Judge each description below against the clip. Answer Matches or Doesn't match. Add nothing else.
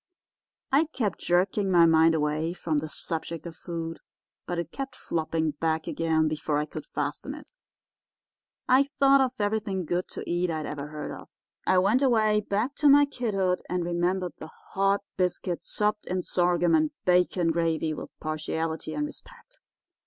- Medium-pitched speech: Matches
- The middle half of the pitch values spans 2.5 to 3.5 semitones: Doesn't match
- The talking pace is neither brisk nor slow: Matches